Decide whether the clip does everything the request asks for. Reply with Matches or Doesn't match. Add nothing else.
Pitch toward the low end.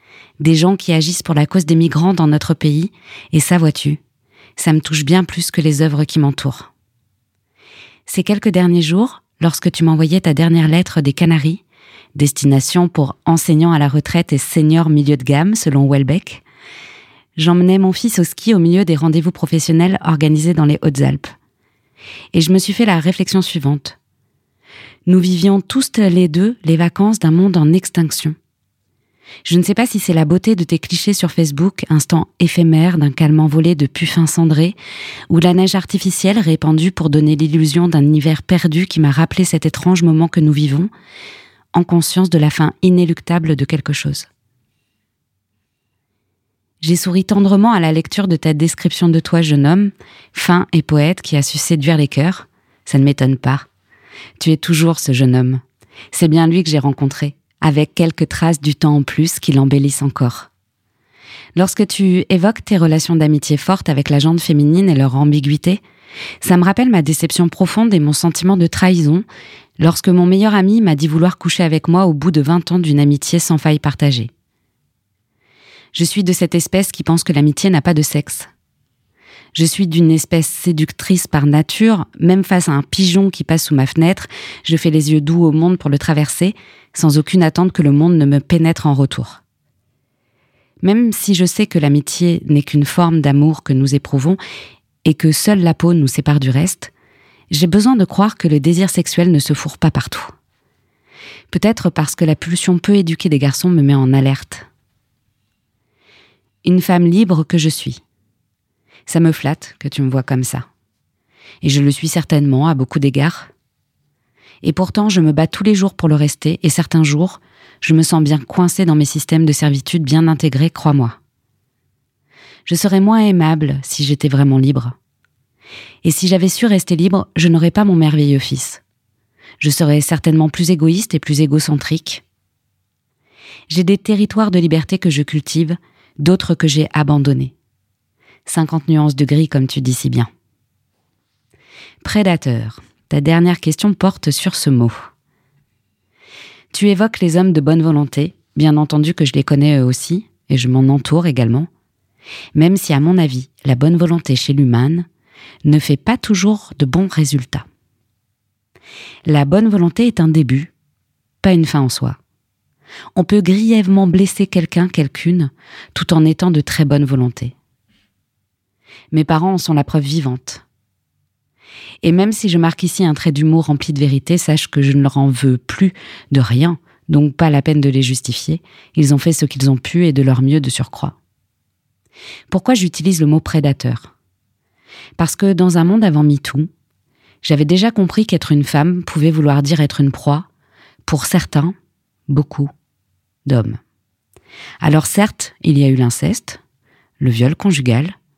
Doesn't match